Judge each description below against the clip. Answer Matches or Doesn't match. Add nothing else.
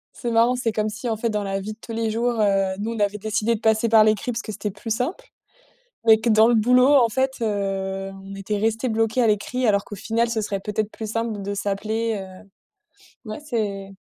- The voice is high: Matches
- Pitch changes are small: Matches